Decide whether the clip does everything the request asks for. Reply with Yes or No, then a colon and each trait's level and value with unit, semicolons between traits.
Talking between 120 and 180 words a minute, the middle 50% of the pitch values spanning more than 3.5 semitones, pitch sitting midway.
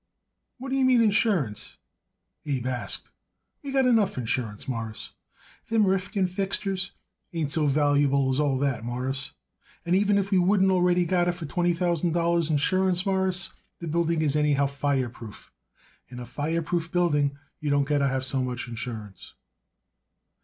Yes: average, 155 wpm; wide, 5.5 semitones; medium, 160 Hz